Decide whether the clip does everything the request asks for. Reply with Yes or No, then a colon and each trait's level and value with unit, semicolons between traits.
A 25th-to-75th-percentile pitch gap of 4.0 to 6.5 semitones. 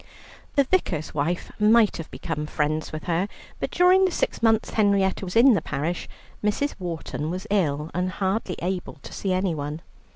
Yes: average, 5.1 semitones